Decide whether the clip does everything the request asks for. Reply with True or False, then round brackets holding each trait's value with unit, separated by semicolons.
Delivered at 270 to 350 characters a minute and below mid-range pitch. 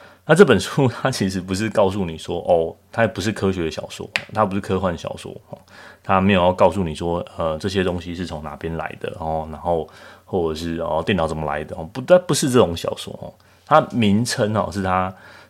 True (300 characters per minute; 95 Hz)